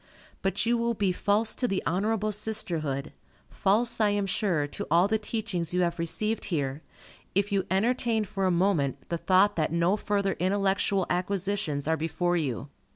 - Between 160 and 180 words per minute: Yes, average, 170 wpm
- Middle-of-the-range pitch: No, high, 195 Hz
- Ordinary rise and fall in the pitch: Yes, average, 3.5 semitones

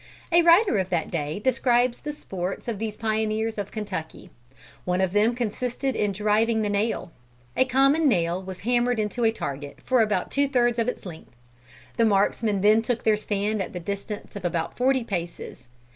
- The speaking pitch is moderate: No, high, 215 Hz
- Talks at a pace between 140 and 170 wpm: No, average, 185 wpm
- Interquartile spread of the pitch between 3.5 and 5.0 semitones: Yes, average, 4.0 semitones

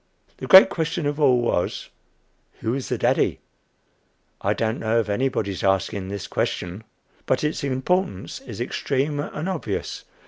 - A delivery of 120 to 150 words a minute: Yes, average, 145 wpm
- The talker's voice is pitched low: Yes, low, 130 Hz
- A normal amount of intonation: No, wide, 6.2 semitones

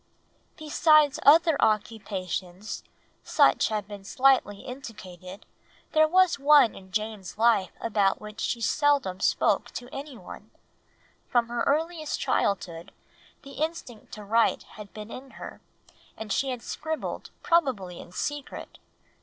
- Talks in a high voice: Yes, high, 230 Hz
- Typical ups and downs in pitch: No, wide, 6.1 semitones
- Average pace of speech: No, slow, 130 wpm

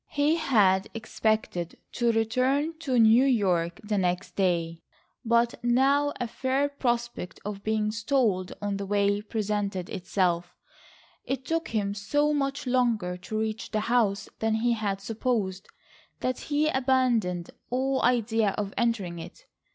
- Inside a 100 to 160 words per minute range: Yes, average, 140 wpm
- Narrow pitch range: No, average, 4.4 semitones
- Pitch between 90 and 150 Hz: No, high, 220 Hz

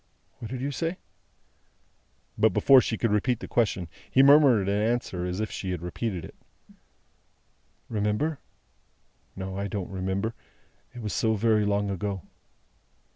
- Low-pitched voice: Yes, low, 105 Hz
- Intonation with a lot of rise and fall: No, average, 3.8 semitones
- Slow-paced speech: No, average, 145 wpm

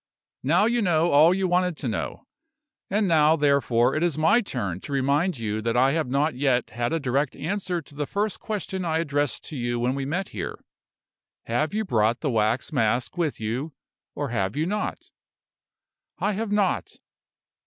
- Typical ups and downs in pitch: No, wide, 6.4 semitones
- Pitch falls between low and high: Yes, medium, 145 Hz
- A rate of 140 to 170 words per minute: No, average, 185 wpm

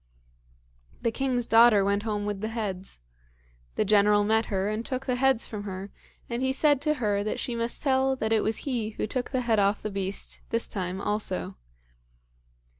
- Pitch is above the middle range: Yes, high, 220 Hz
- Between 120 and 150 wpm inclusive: No, average, 190 wpm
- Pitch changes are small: No, average, 3.4 semitones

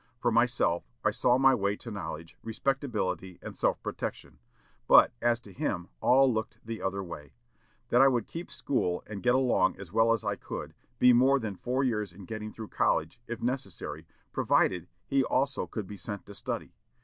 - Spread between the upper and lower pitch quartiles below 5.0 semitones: Yes, average, 4.3 semitones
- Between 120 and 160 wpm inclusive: No, average, 185 wpm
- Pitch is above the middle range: No, low, 115 Hz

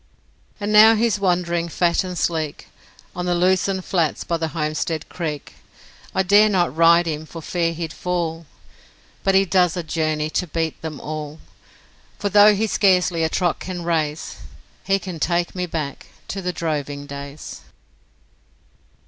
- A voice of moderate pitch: Yes, medium, 170 Hz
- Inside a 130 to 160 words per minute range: Yes, average, 155 wpm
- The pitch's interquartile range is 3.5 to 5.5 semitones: No, average, 2.8 semitones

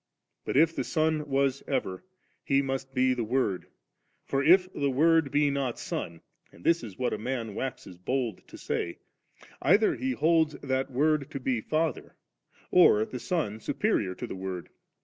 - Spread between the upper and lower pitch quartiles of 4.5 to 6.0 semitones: Yes, average, 4.9 semitones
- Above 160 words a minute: Yes, average, 170 wpm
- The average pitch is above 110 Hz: Yes, low, 135 Hz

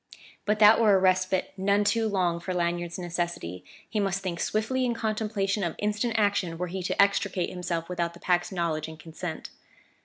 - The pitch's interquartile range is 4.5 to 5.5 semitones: No, average, 3.2 semitones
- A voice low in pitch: No, medium, 185 Hz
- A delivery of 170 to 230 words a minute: Yes, average, 185 wpm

